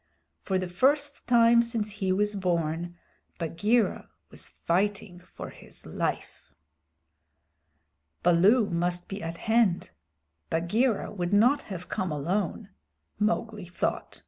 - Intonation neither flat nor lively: Yes, average, 4.2 semitones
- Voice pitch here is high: Yes, high, 195 Hz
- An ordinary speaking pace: No, slow, 115 wpm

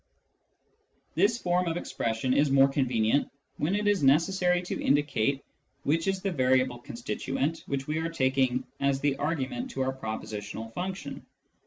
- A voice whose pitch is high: No, medium, 140 Hz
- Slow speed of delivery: No, average, 150 wpm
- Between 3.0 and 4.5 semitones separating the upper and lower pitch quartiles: No, average, 5.0 semitones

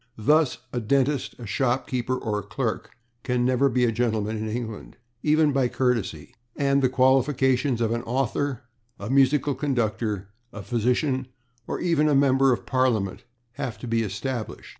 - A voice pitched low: Yes, low, 125 Hz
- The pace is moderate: Yes, average, 160 wpm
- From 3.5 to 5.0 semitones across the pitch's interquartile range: No, average, 3.1 semitones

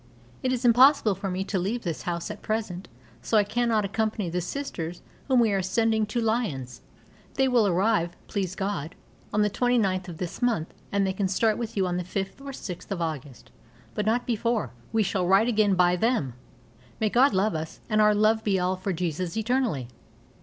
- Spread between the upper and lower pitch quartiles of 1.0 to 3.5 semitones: No, average, 3.9 semitones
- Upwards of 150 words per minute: Yes, average, 200 wpm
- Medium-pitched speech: No, high, 200 Hz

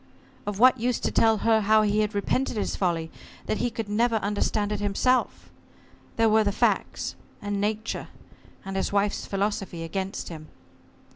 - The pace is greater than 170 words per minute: No, average, 165 wpm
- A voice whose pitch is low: No, high, 210 Hz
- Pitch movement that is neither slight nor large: No, narrow, 1.9 semitones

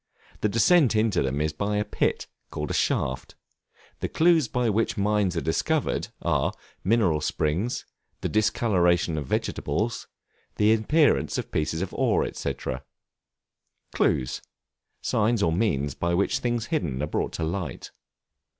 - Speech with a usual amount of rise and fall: No, wide, 6.2 semitones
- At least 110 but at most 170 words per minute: Yes, average, 140 wpm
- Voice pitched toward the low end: Yes, low, 100 Hz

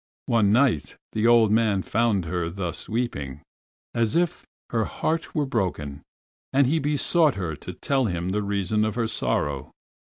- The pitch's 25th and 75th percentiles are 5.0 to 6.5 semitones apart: Yes, wide, 5.4 semitones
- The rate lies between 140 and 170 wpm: Yes, average, 160 wpm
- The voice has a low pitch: Yes, low, 110 Hz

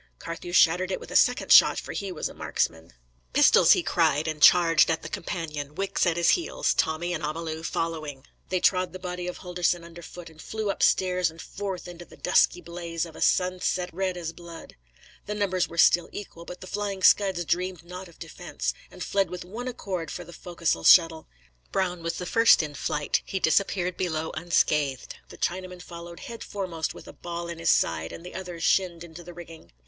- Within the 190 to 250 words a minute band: Yes, average, 200 wpm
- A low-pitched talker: No, medium, 175 Hz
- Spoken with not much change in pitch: Yes, narrow, 1.9 semitones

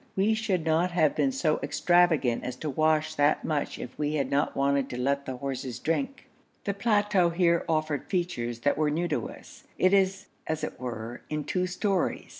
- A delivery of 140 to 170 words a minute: No, average, 195 wpm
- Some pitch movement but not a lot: Yes, average, 4.7 semitones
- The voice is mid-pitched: Yes, medium, 155 Hz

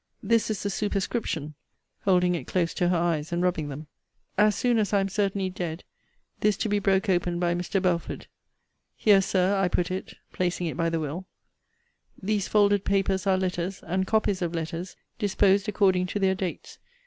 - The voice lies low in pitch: No, medium, 185 Hz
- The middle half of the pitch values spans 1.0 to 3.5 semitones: Yes, narrow, 2.4 semitones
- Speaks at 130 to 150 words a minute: No, average, 185 wpm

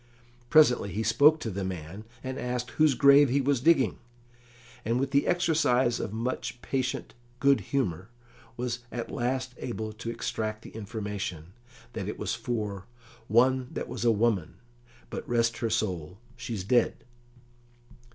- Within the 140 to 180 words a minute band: Yes, average, 150 wpm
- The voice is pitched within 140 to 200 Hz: No, low, 120 Hz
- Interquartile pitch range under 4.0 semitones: Yes, average, 3.4 semitones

